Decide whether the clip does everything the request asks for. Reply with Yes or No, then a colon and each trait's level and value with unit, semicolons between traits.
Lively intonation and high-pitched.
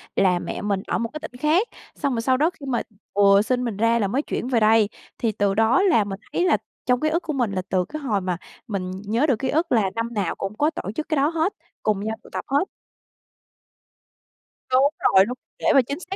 Yes: wide, 6.1 semitones; high, 235 Hz